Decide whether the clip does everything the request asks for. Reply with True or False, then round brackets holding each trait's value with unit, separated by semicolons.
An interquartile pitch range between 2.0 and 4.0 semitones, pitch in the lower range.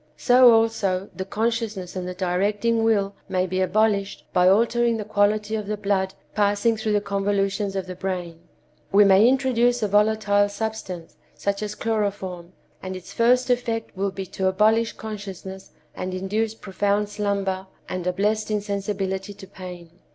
False (2.4 semitones; 205 Hz)